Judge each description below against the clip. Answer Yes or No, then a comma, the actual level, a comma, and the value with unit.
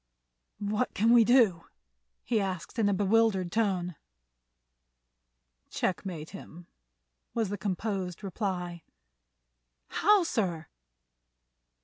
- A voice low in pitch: No, high, 195 Hz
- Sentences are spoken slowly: Yes, slow, 90 wpm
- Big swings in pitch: No, average, 3.9 semitones